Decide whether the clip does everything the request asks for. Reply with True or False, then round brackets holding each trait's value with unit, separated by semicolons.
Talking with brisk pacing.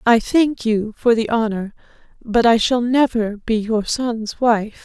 False (175 wpm)